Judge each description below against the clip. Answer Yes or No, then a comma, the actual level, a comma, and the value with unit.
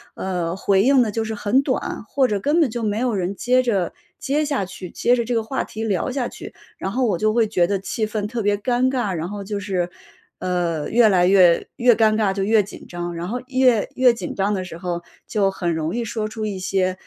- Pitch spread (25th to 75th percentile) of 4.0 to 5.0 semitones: Yes, average, 4.3 semitones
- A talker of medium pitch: No, high, 210 Hz